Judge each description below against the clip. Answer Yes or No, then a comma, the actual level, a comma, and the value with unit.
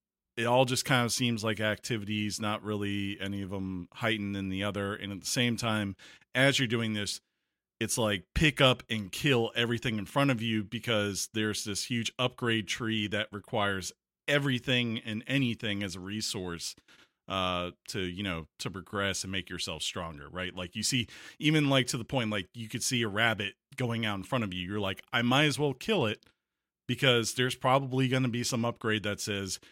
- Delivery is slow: No, average, 200 wpm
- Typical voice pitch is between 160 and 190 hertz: No, low, 110 Hz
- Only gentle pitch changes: No, average, 3.8 semitones